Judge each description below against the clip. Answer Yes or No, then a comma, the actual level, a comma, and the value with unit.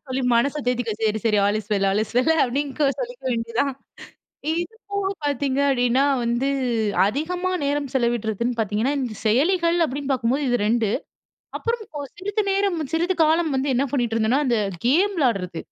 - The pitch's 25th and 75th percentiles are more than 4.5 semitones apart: Yes, wide, 5.5 semitones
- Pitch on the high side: Yes, very high, 265 Hz